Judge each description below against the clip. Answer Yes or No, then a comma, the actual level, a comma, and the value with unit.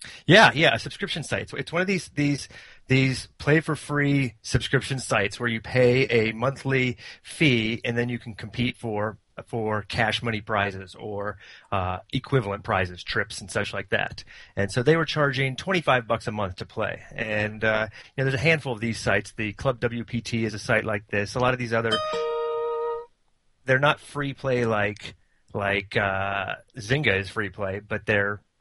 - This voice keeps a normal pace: Yes, average, 195 wpm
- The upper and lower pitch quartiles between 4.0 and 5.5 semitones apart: Yes, average, 4.3 semitones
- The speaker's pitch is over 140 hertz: No, low, 120 Hz